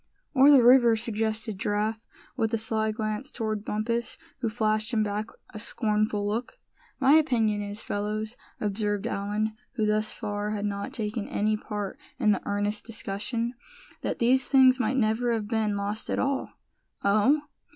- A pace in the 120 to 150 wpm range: No, average, 160 wpm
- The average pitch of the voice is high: Yes, high, 215 Hz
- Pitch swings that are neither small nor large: No, narrow, 2.0 semitones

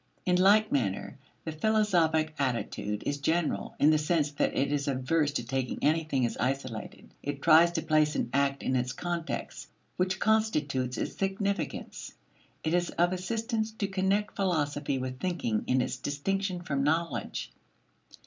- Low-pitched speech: No, medium, 155 Hz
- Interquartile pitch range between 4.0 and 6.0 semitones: Yes, average, 5.0 semitones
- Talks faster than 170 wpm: No, average, 155 wpm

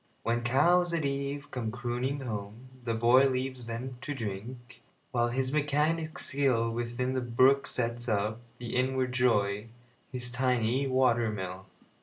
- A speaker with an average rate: No, slow, 130 wpm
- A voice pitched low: Yes, low, 125 Hz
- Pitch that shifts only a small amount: Yes, narrow, 2.3 semitones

